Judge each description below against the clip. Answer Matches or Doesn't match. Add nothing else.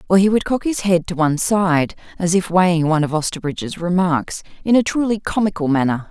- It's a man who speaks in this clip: Doesn't match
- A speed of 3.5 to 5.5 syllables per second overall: Doesn't match